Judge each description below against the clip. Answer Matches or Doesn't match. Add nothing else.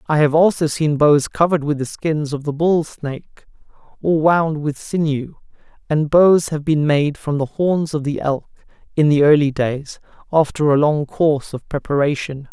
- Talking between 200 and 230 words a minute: Doesn't match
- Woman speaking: Doesn't match